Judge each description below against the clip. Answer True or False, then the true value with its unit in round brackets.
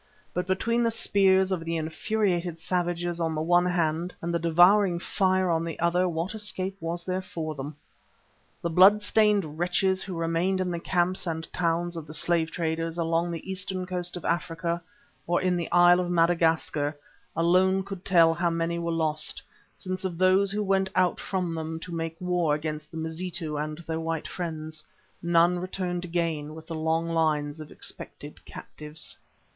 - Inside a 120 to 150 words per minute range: False (175 wpm)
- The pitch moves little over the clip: True (2.1 semitones)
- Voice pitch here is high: False (170 Hz)